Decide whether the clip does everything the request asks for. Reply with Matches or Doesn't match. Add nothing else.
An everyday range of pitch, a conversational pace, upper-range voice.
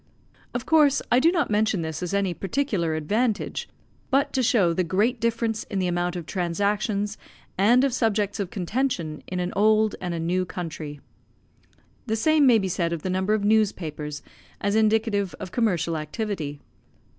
Matches